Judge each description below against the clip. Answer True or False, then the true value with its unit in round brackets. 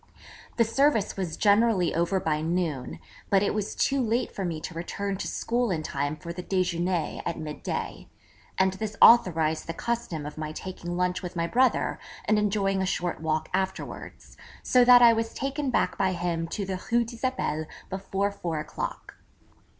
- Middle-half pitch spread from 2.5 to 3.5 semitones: False (4.8 semitones)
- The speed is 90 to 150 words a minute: False (180 wpm)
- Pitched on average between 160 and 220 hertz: True (185 Hz)